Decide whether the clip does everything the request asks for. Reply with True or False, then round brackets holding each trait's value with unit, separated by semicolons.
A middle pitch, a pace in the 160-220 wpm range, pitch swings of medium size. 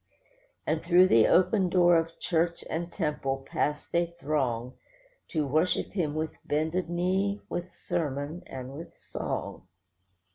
False (165 Hz; 135 wpm; 3.1 semitones)